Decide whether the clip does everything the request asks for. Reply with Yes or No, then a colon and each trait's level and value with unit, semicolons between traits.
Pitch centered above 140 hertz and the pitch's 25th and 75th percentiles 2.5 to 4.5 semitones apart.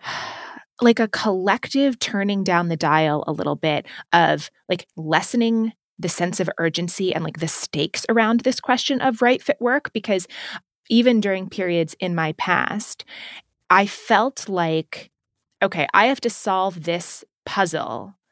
No: high, 190 Hz; wide, 5.6 semitones